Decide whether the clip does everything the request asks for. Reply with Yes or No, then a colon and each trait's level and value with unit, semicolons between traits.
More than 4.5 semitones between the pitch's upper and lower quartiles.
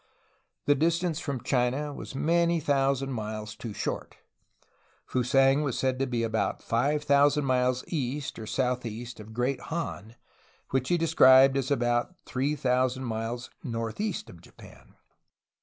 No: average, 3.2 semitones